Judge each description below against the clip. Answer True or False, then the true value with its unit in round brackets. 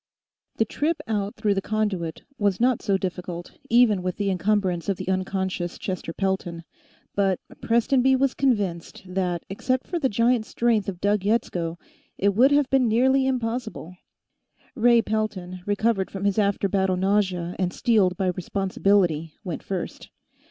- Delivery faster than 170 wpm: False (150 wpm)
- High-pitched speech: True (200 Hz)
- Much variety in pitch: False (3.8 semitones)